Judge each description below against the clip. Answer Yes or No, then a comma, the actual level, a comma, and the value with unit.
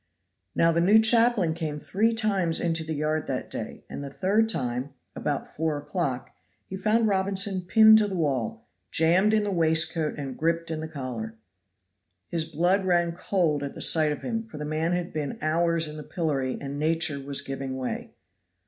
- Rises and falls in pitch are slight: No, average, 4.3 semitones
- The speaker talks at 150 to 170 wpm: No, average, 185 wpm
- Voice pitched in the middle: Yes, medium, 165 Hz